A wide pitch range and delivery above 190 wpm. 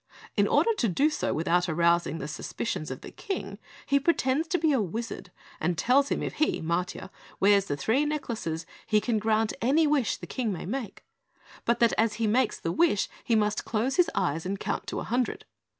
Yes: wide, 6.9 semitones; fast, 205 wpm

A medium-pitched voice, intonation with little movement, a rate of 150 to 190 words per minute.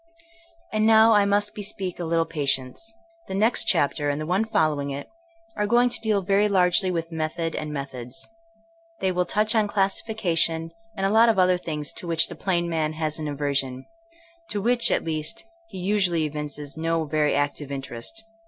No: medium, 170 Hz; average, 5.2 semitones; average, 180 wpm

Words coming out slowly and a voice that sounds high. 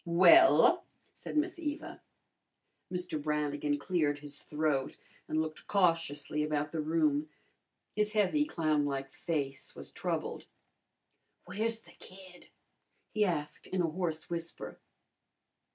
No: slow, 115 wpm; medium, 160 Hz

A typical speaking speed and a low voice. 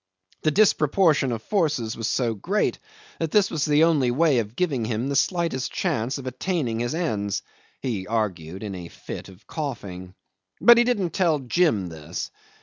Yes: average, 165 wpm; low, 130 Hz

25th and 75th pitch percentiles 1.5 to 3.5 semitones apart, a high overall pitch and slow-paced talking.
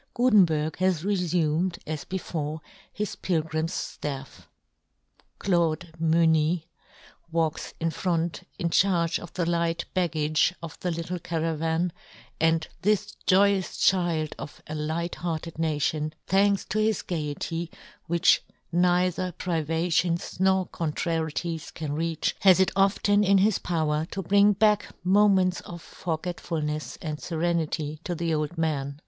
No: narrow, 2.5 semitones; medium, 170 Hz; slow, 125 wpm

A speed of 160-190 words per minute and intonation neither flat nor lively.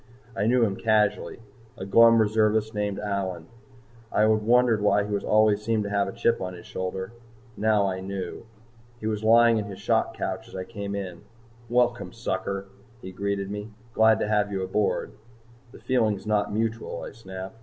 No: average, 180 wpm; narrow, 2.0 semitones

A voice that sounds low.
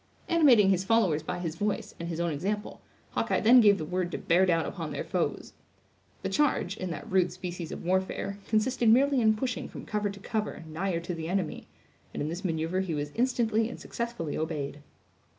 No: high, 190 Hz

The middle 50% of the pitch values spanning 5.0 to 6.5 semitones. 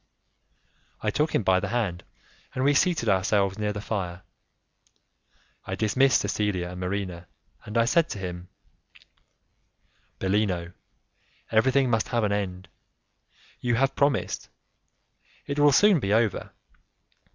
Yes: wide, 5.4 semitones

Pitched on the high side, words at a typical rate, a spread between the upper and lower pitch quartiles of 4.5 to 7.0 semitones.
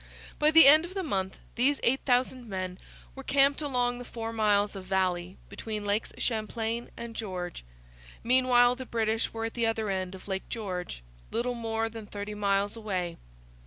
No: high, 225 Hz; average, 170 wpm; average, 3.7 semitones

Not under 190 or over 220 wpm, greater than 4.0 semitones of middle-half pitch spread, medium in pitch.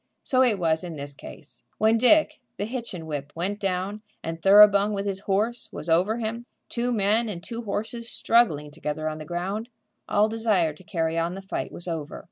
No: average, 195 wpm; average, 5.1 semitones; high, 195 Hz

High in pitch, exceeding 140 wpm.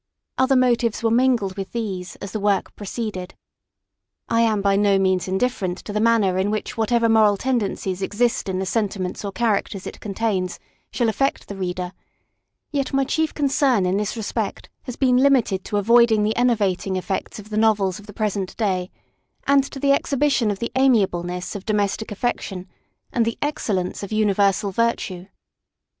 Yes: high, 210 Hz; average, 175 wpm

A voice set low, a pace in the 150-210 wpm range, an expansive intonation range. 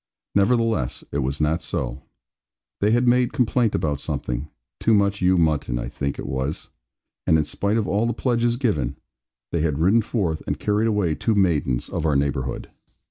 Yes: very low, 85 Hz; average, 180 wpm; wide, 7.6 semitones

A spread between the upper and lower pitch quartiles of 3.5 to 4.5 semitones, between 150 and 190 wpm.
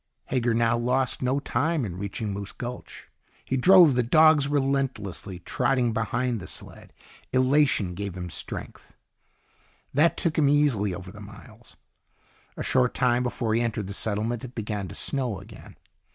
Yes: average, 4.2 semitones; average, 160 wpm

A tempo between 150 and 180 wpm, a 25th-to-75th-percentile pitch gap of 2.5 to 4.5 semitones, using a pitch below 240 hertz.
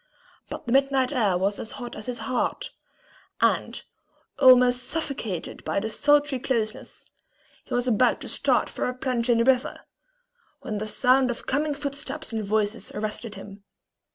No: average, 160 wpm; average, 3.6 semitones; high, 245 Hz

